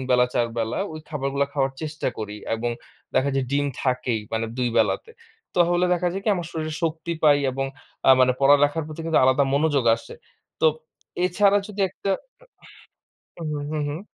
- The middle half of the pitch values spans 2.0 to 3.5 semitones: No, average, 3.9 semitones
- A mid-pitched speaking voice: Yes, medium, 145 Hz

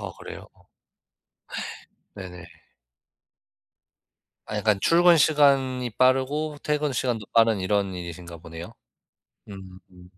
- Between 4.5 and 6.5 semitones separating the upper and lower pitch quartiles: No, wide, 6.9 semitones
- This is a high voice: No, low, 110 Hz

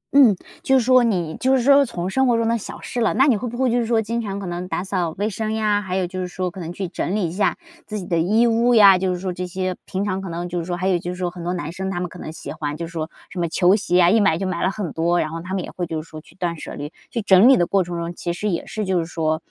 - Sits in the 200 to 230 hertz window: No, medium, 185 Hz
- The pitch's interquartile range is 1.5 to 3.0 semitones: No, average, 3.7 semitones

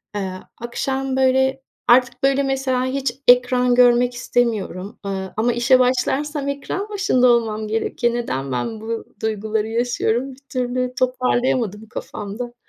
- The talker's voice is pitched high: Yes, high, 245 Hz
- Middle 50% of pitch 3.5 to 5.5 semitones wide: No, average, 2.8 semitones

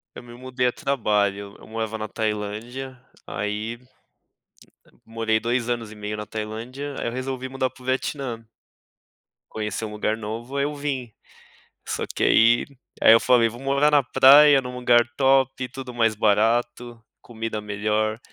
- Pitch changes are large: No, average, 3.1 semitones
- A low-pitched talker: Yes, low, 120 Hz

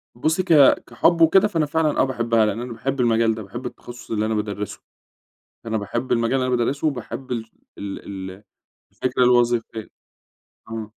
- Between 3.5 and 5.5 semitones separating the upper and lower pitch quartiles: No, average, 3.1 semitones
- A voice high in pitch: No, low, 120 Hz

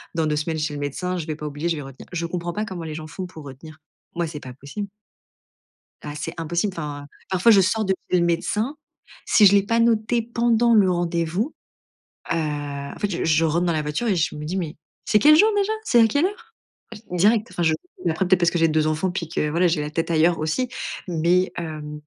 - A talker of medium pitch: Yes, medium, 170 Hz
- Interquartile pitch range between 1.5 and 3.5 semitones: No, average, 4.6 semitones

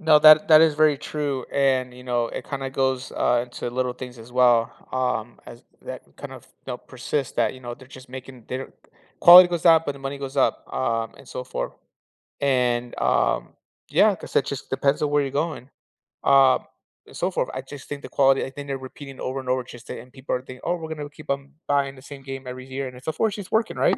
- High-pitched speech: No, low, 135 Hz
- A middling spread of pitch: No, narrow, 2.3 semitones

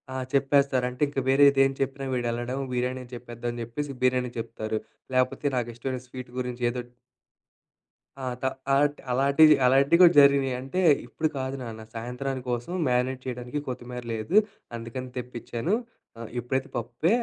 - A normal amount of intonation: No, narrow, 2.1 semitones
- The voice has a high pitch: No, low, 130 Hz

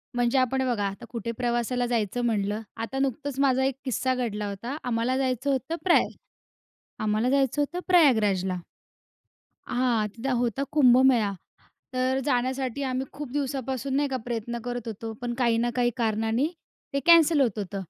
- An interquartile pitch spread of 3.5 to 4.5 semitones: No, average, 2.8 semitones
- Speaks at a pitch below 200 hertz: No, high, 245 Hz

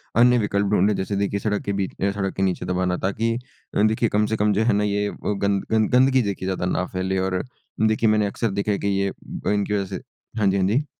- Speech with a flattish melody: Yes, narrow, 1.8 semitones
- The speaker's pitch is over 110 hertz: No, low, 100 Hz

